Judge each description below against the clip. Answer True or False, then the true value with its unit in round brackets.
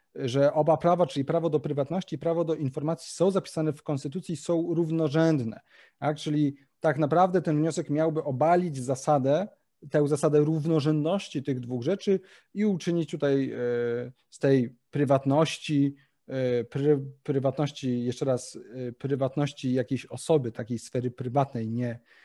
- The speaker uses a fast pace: False (140 wpm)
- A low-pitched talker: False (150 Hz)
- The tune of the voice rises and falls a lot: False (3.3 semitones)